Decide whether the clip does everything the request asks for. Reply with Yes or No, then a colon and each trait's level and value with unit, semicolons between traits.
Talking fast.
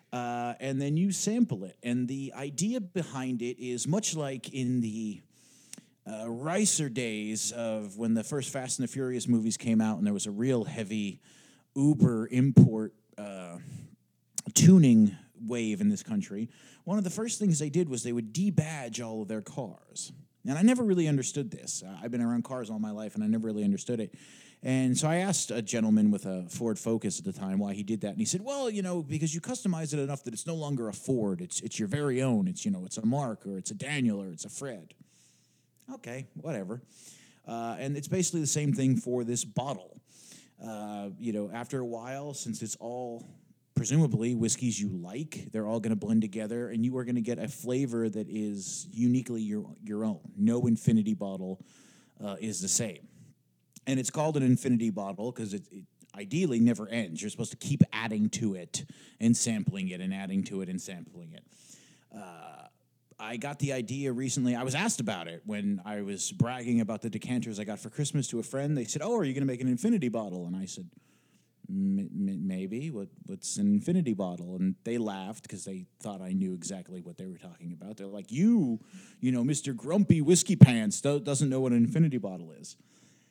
Yes: fast, 210 wpm